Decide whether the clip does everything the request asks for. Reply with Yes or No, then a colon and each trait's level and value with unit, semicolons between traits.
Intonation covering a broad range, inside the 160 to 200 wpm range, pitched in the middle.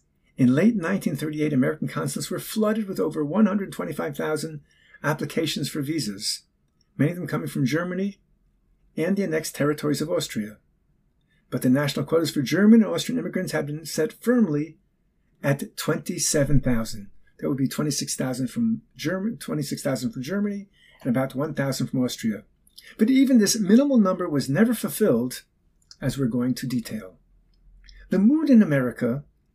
No: wide, 8.3 semitones; average, 145 wpm; medium, 155 Hz